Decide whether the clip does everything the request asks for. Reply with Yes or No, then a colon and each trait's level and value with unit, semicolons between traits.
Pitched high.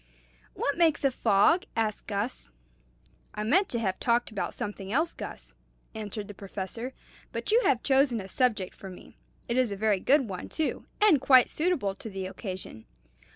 Yes: high, 225 Hz